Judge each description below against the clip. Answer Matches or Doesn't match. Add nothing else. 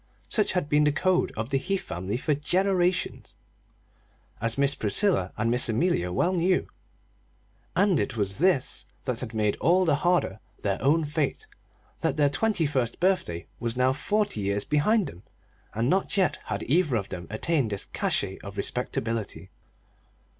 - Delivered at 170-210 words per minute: Doesn't match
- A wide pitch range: Matches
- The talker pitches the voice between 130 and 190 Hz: Matches